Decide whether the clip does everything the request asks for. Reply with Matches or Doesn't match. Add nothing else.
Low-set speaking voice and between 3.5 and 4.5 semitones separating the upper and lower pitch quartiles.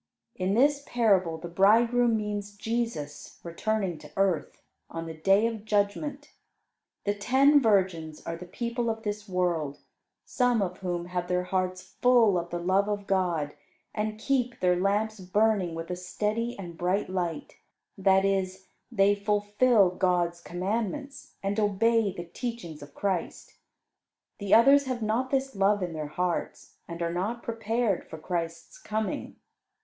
Doesn't match